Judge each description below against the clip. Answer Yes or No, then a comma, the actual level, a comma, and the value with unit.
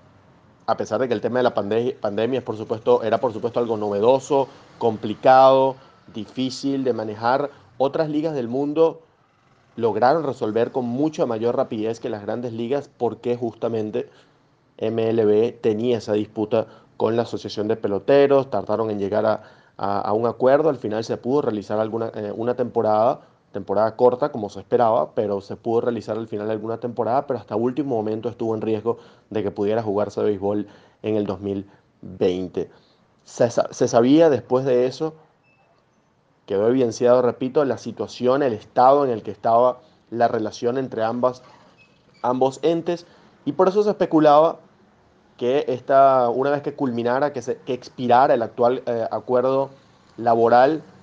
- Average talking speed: Yes, average, 160 wpm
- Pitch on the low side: Yes, low, 120 Hz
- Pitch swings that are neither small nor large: Yes, average, 3.7 semitones